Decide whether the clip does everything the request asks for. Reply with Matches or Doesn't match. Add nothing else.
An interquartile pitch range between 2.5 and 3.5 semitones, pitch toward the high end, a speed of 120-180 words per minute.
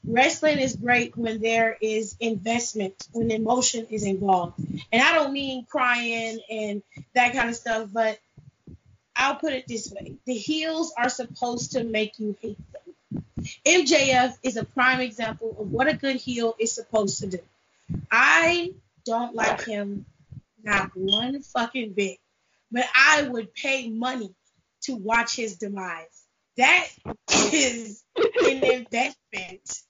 Matches